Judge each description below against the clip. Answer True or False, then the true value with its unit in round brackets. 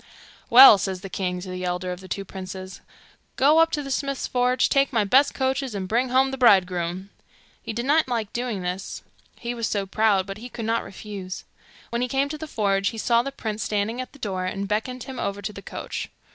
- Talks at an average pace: False (230 wpm)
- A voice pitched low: False (220 Hz)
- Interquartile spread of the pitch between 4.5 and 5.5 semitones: True (4.9 semitones)